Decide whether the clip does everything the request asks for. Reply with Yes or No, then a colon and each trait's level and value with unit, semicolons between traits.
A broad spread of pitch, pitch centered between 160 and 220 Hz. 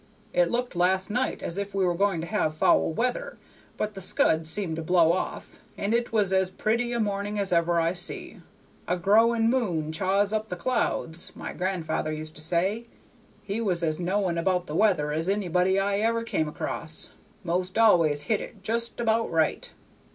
No: average, 4.3 semitones; high, 190 Hz